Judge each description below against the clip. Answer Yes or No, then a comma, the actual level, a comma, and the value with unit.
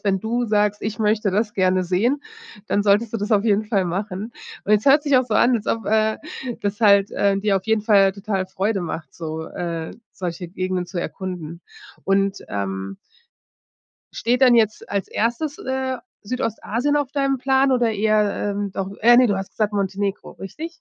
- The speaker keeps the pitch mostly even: No, average, 3.1 semitones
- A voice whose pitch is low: No, high, 205 Hz